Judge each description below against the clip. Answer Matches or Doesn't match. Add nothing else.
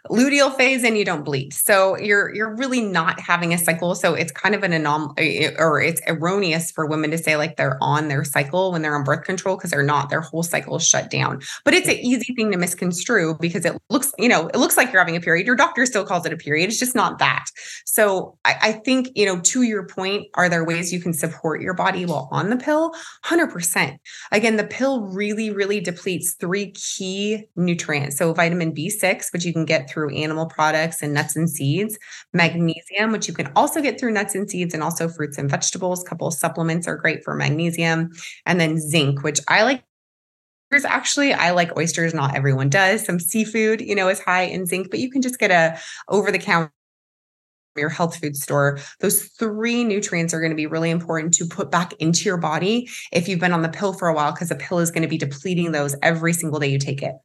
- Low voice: Doesn't match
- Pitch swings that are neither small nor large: Matches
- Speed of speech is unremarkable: Doesn't match